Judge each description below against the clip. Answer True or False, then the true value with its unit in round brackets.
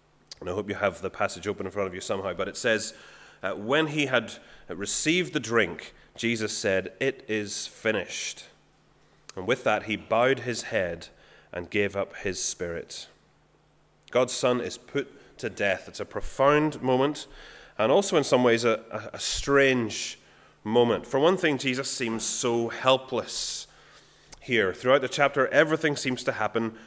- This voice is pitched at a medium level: False (125 Hz)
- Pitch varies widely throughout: False (4.3 semitones)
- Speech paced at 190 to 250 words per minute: False (165 wpm)